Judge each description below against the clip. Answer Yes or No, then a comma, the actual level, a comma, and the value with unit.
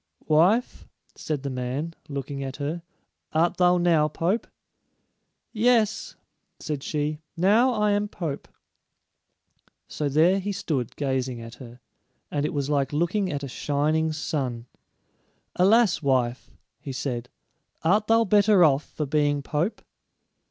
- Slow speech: Yes, slow, 130 wpm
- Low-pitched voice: No, medium, 155 Hz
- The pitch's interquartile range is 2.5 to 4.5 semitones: No, average, 5.1 semitones